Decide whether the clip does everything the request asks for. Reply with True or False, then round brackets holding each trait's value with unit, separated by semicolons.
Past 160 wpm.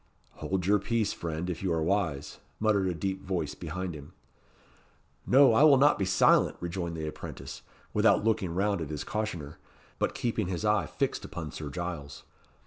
True (175 wpm)